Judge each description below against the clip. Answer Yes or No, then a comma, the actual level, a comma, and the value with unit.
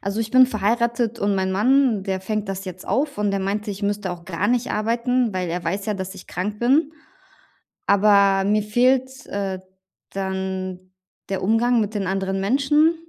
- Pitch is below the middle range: No, high, 205 Hz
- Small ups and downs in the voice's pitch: No, average, 3.7 semitones